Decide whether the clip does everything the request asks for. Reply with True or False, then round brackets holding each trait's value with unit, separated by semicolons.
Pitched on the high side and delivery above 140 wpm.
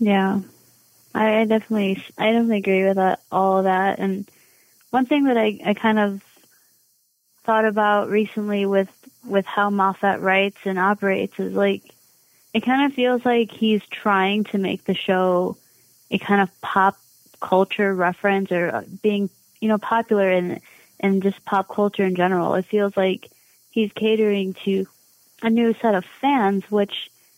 True (200 Hz; 160 wpm)